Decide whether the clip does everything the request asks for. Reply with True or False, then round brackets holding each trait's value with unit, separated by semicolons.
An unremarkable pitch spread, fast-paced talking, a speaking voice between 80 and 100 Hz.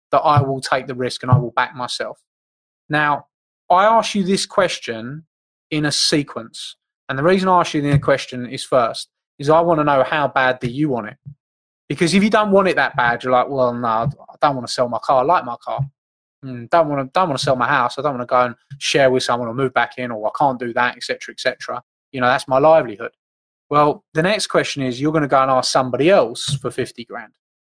False (4.0 semitones; 255 wpm; 135 Hz)